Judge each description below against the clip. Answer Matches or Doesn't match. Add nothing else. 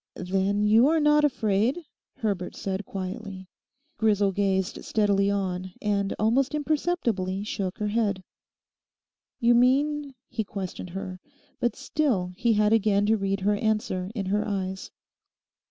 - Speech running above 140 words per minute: Doesn't match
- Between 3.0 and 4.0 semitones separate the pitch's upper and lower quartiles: Matches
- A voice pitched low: Doesn't match